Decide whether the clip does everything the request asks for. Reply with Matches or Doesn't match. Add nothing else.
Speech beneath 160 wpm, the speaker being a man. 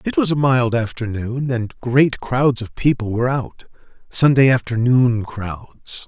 Matches